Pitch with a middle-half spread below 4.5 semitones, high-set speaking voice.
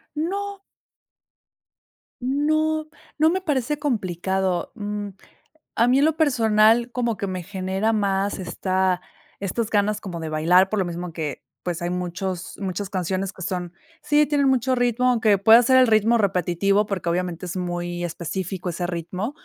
No: average, 5.3 semitones; high, 200 Hz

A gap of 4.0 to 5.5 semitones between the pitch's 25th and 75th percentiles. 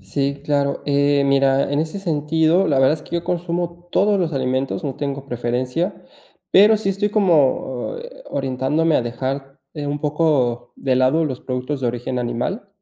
Yes: average, 4.3 semitones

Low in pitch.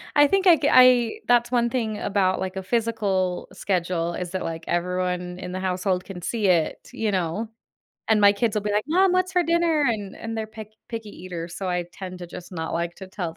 No: high, 195 Hz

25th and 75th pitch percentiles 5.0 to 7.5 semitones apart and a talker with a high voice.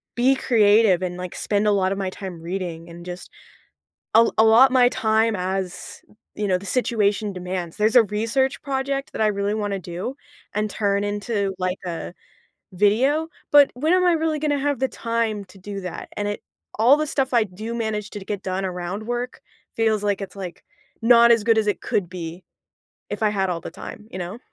No: average, 3.8 semitones; high, 210 Hz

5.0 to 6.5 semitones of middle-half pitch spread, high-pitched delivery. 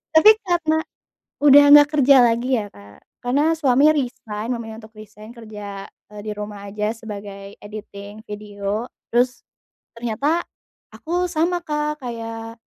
Yes: wide, 5.6 semitones; high, 230 Hz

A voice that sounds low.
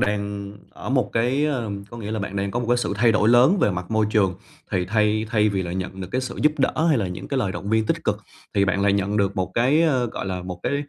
Yes: low, 105 Hz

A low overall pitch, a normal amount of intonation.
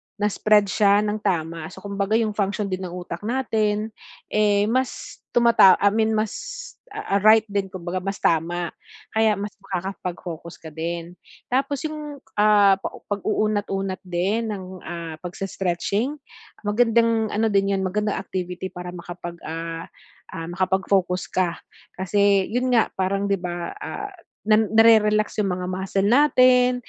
No: high, 200 Hz; average, 3.2 semitones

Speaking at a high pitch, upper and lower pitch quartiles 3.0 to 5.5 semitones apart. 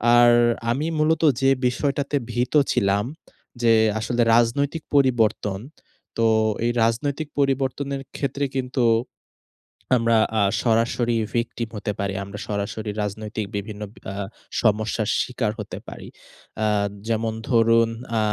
No: low, 115 Hz; average, 3.4 semitones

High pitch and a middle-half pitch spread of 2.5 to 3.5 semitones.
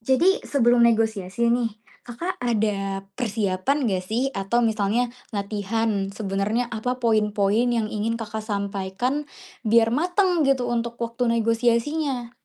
Yes: high, 230 Hz; average, 3.0 semitones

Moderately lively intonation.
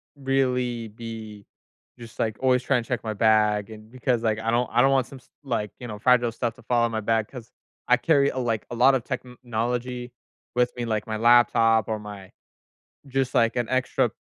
No: narrow, 2.2 semitones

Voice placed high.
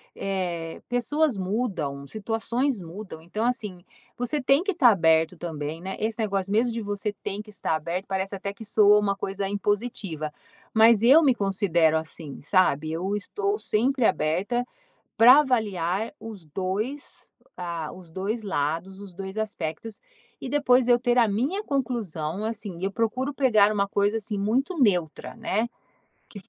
Yes: high, 205 Hz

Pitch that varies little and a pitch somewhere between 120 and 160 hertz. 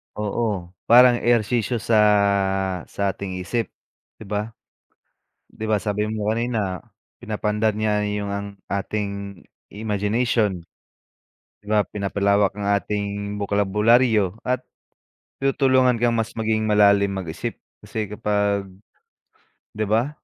No: narrow, 1.8 semitones; low, 105 Hz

